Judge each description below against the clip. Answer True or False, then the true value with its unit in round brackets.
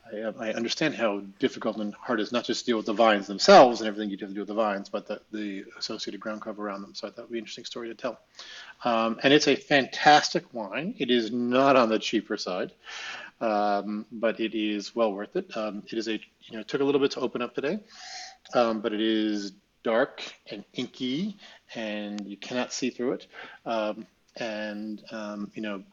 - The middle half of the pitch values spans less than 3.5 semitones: True (2.8 semitones)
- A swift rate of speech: True (215 wpm)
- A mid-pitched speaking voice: False (110 Hz)